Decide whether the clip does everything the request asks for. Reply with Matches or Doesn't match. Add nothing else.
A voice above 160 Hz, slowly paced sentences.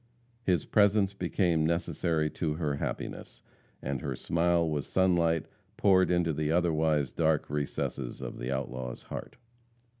Doesn't match